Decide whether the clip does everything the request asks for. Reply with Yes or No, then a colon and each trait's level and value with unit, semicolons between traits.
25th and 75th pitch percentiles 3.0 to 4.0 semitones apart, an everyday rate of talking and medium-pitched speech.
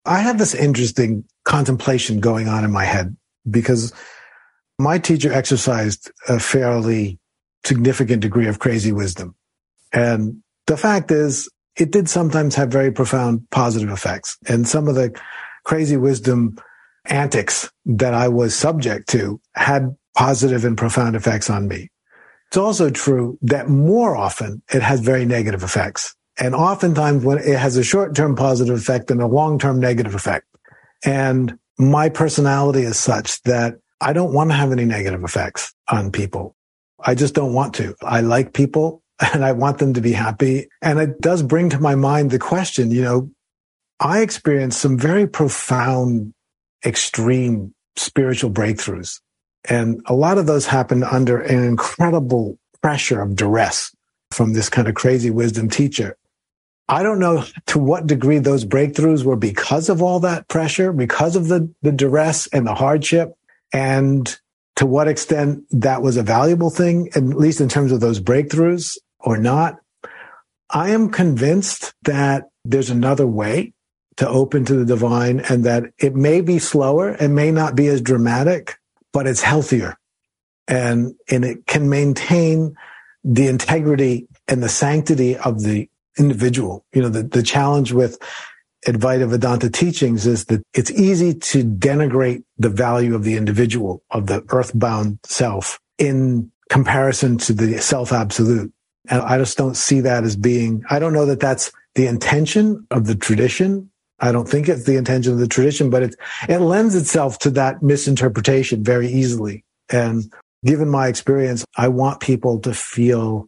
No: average, 3.7 semitones; average, 160 wpm; low, 130 Hz